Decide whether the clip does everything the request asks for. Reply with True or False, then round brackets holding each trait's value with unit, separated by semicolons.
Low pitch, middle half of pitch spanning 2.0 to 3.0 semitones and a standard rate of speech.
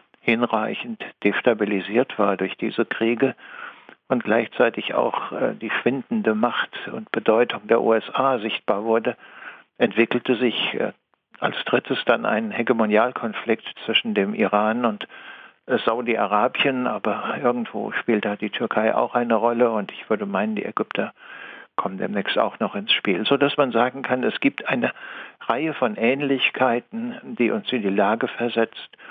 True (120 Hz; 2.5 semitones; 140 wpm)